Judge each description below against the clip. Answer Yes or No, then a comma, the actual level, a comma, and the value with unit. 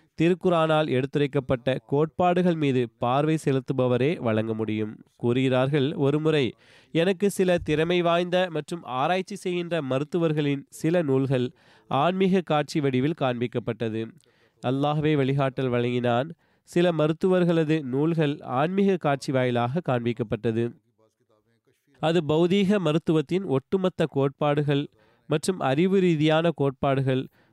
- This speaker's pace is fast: No, average, 95 wpm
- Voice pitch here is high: No, medium, 145 Hz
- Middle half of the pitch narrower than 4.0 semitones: No, average, 4.7 semitones